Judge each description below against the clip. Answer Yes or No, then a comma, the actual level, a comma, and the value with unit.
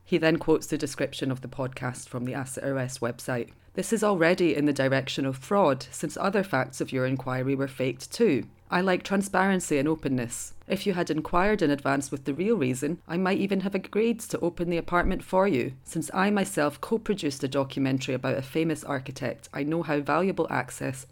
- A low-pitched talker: No, medium, 145 Hz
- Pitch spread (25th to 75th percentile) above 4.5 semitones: Yes, average, 5.2 semitones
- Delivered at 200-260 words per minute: Yes, fast, 205 wpm